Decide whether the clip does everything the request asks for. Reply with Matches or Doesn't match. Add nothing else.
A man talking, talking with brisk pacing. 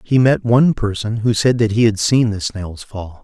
Matches